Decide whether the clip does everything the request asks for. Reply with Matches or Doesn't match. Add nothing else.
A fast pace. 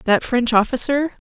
Doesn't match